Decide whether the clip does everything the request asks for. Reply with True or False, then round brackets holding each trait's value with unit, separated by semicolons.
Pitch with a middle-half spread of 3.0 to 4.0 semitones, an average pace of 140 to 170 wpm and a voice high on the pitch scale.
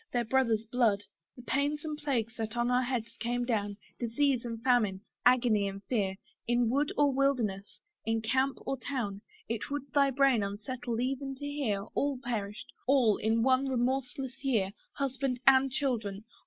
True (3.4 semitones; 165 wpm; 245 Hz)